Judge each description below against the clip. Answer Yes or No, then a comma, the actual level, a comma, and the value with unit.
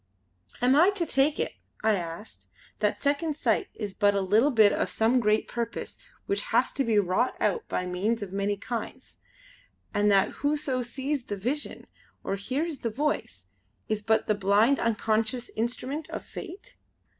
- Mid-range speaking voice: No, high, 230 Hz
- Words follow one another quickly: No, average, 170 wpm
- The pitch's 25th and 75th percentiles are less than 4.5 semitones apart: No, wide, 5.5 semitones